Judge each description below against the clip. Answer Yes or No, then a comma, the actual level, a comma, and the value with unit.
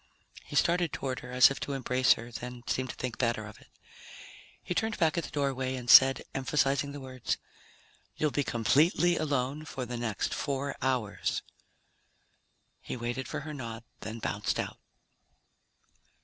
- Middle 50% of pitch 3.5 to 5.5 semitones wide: No, average, 2.9 semitones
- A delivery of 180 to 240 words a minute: No, average, 165 wpm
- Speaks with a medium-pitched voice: No, low, 130 Hz